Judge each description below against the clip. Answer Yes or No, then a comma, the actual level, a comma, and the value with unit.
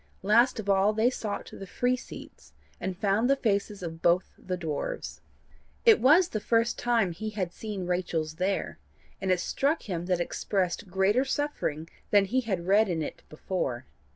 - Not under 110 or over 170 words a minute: No, average, 180 wpm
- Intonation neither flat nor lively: Yes, average, 4.3 semitones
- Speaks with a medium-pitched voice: No, high, 195 Hz